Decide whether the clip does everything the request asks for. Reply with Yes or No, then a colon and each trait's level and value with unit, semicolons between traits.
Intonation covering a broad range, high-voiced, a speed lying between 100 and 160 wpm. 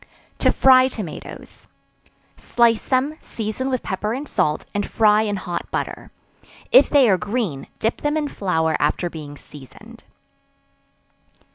Yes: wide, 6.7 semitones; high, 215 Hz; slow, 135 wpm